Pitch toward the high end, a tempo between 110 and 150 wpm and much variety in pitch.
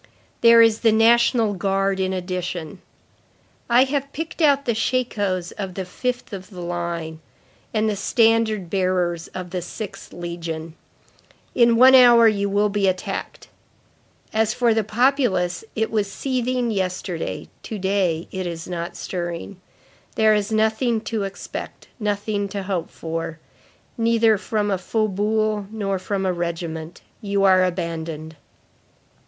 No: high, 200 Hz; average, 140 wpm; average, 3.8 semitones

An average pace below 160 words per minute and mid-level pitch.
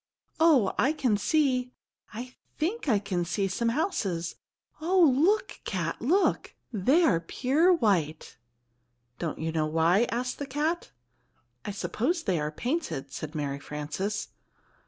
No: slow, 135 wpm; high, 220 Hz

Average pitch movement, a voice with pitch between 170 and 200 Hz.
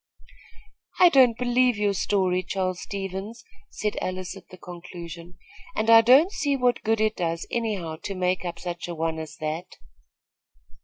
Yes: average, 4.5 semitones; high, 190 Hz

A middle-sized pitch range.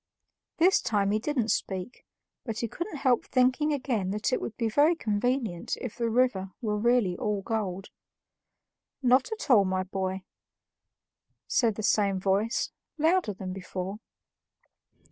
Yes: average, 4.7 semitones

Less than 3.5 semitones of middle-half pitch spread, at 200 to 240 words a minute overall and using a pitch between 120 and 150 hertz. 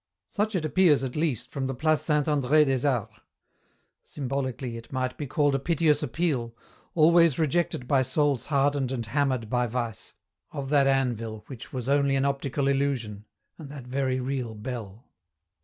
No: average, 2.9 semitones; average, 165 wpm; low, 135 Hz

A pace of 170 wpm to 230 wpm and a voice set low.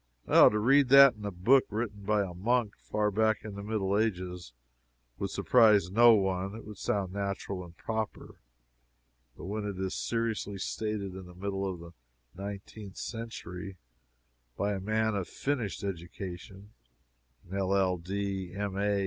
No: average, 155 wpm; low, 100 Hz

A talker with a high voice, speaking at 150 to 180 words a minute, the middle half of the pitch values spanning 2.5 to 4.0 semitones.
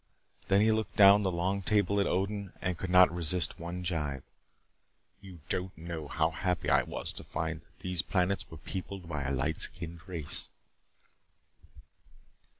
No: very low, 90 Hz; average, 160 wpm; average, 2.8 semitones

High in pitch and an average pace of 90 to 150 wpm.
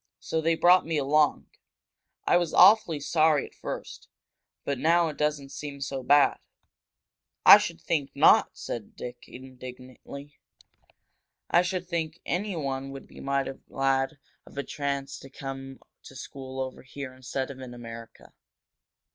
No: medium, 140 Hz; average, 145 wpm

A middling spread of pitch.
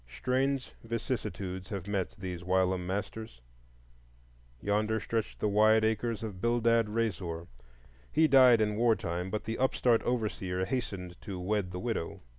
Yes: average, 3.8 semitones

